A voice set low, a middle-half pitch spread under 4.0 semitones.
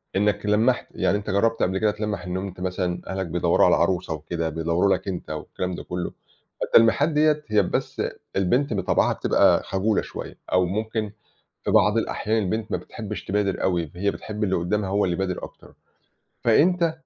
Yes: low, 100 Hz; average, 3.3 semitones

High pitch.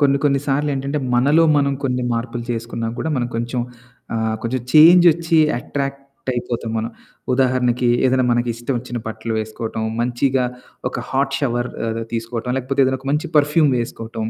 No: low, 125 Hz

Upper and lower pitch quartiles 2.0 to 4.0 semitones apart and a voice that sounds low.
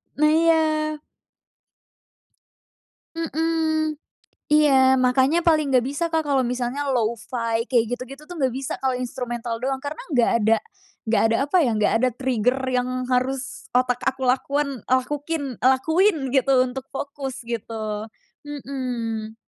No: average, 3.1 semitones; very high, 265 Hz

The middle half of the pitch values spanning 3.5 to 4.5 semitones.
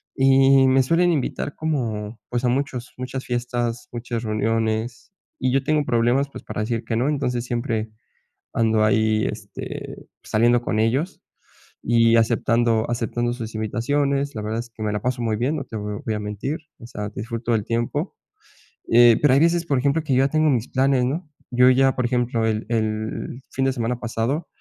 No: average, 2.9 semitones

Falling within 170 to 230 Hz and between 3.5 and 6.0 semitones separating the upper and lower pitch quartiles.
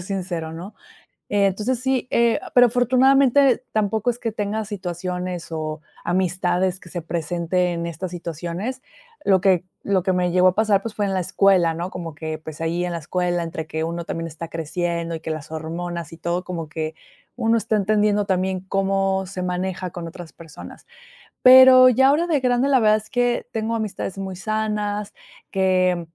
Yes: medium, 185 Hz; average, 4.0 semitones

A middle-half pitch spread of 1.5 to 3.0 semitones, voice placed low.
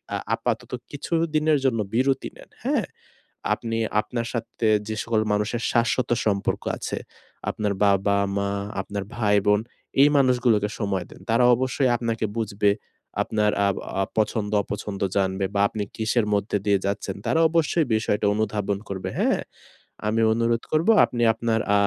Yes: average, 2.7 semitones; low, 110 Hz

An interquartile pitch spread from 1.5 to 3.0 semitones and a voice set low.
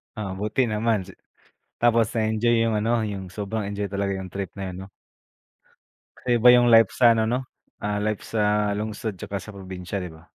Yes: narrow, 2.5 semitones; low, 105 Hz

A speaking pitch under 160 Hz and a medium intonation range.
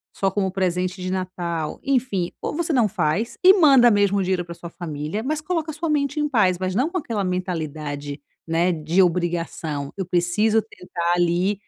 No: medium, 185 Hz; average, 5.0 semitones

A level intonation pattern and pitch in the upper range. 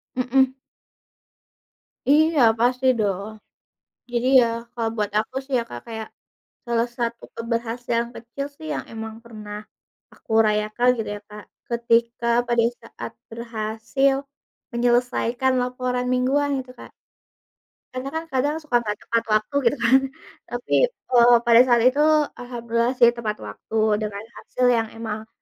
Yes: narrow, 2.1 semitones; high, 235 Hz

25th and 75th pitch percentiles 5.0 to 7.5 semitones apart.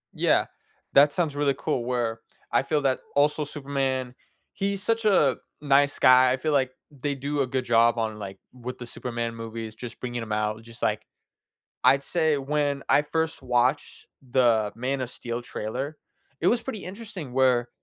No: average, 3.5 semitones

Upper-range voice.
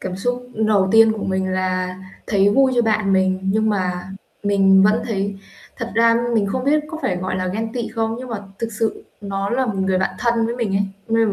Yes: high, 210 Hz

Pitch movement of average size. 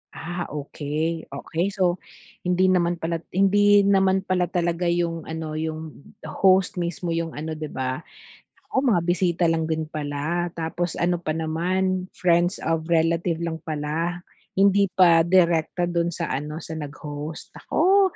No: narrow, 2.2 semitones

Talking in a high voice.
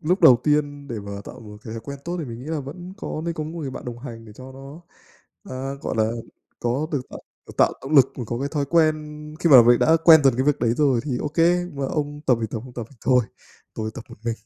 No: low, 135 Hz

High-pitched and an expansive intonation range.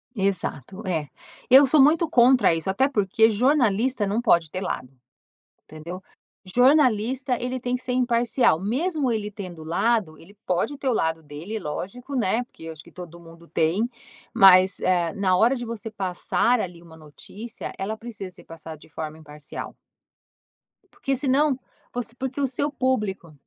Yes: high, 210 Hz; wide, 6.5 semitones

